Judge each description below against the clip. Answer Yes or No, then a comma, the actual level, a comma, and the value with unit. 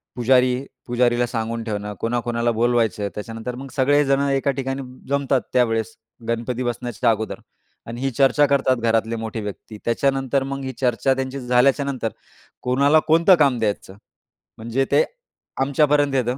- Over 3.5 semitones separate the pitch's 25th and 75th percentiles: No, average, 2.8 semitones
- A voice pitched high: No, low, 125 Hz